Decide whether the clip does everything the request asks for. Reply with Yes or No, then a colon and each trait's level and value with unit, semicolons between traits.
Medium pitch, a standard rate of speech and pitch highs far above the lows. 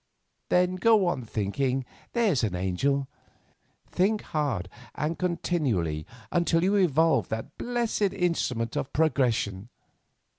No: medium, 150 Hz; slow, 110 wpm; wide, 7.9 semitones